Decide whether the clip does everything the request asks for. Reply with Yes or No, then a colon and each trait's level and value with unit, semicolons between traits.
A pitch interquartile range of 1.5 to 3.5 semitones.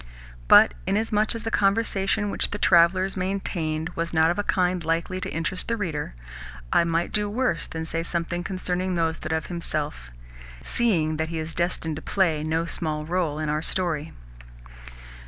Yes: average, 3.0 semitones